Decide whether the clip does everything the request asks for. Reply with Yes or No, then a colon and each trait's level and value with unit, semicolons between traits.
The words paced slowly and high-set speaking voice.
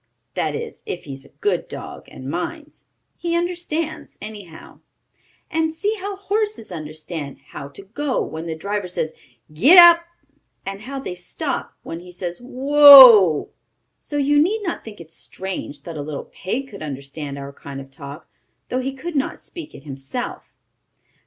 No: average, 165 wpm; high, 210 Hz